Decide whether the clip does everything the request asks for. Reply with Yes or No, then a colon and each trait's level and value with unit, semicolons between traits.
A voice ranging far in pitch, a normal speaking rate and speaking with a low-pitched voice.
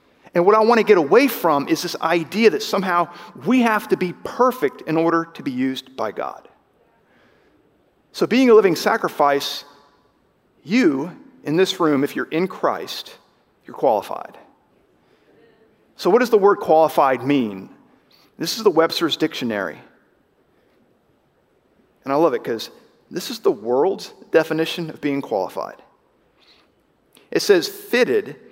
No: wide, 6.4 semitones; average, 145 wpm; medium, 175 Hz